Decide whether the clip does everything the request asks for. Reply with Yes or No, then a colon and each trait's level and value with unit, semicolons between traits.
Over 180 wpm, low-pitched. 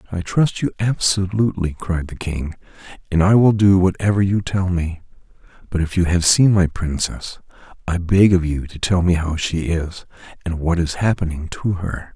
Yes: average, 190 wpm; very low, 90 Hz